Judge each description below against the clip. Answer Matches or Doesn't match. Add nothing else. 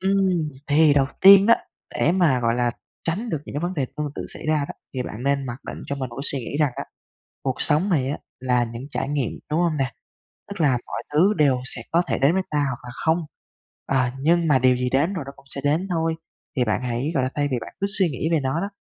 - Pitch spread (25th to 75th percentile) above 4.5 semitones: Doesn't match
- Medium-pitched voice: Matches